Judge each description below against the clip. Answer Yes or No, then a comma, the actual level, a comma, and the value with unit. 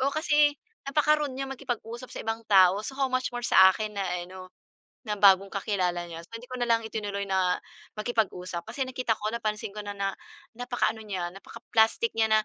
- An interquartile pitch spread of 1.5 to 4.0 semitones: No, average, 4.4 semitones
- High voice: Yes, high, 215 Hz